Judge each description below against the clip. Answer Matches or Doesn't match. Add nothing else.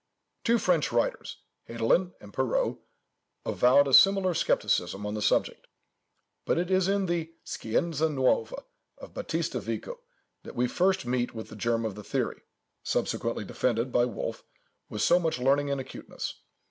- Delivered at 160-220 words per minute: Doesn't match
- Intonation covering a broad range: Matches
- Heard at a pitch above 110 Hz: Matches